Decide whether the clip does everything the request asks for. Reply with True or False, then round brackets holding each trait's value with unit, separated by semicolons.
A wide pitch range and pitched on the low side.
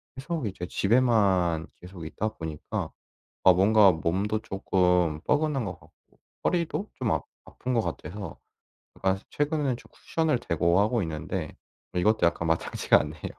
True (6.1 semitones; 100 Hz)